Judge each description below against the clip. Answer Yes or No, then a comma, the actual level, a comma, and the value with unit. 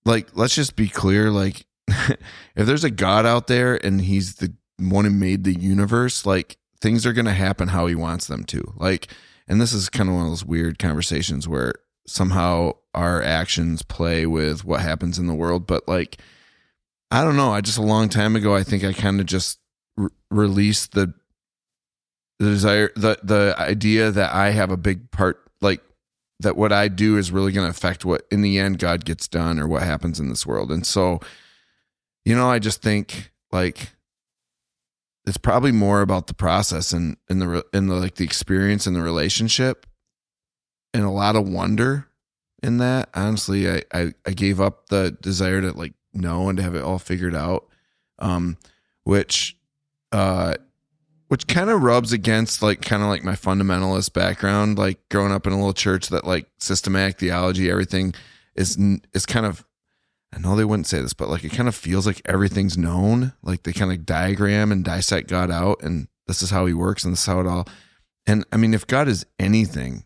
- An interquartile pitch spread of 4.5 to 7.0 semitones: No, average, 3.0 semitones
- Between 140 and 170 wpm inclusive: No, average, 195 wpm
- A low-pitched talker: Yes, very low, 95 Hz